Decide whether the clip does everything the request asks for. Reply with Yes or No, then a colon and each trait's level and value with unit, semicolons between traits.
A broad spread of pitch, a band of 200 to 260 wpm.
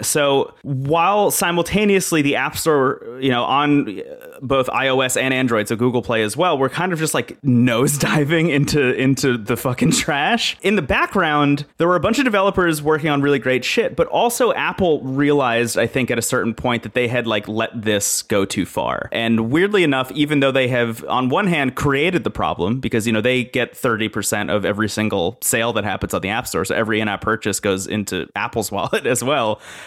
No: average, 4.6 semitones; fast, 205 wpm